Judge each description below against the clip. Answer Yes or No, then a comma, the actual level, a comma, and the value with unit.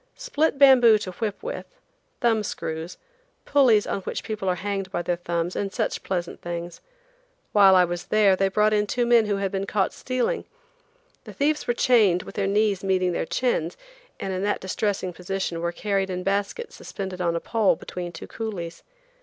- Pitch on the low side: No, high, 195 Hz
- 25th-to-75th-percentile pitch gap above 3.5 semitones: No, average, 3.2 semitones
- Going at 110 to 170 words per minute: No, average, 185 wpm